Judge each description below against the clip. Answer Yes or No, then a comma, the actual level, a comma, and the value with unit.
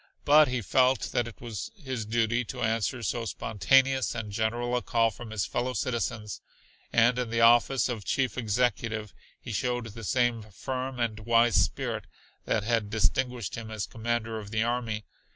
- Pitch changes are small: Yes, narrow, 2.0 semitones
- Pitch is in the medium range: No, low, 115 Hz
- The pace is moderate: Yes, average, 170 wpm